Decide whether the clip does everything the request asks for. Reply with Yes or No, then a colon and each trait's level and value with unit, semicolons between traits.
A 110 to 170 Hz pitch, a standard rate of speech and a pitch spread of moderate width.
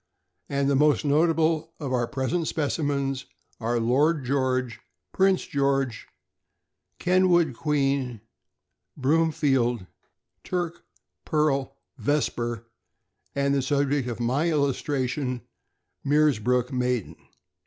No: medium, 140 Hz; slow, 90 wpm; average, 3.2 semitones